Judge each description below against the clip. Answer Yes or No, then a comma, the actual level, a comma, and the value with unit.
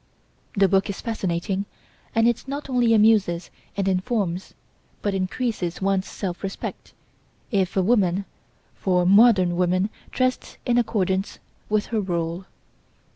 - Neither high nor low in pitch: No, high, 195 Hz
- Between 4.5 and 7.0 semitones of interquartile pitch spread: No, average, 3.4 semitones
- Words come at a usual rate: No, slow, 130 wpm